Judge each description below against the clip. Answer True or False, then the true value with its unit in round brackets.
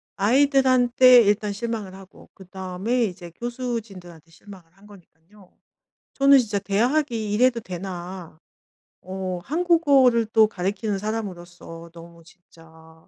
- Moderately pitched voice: False (205 Hz)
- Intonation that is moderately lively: True (4.9 semitones)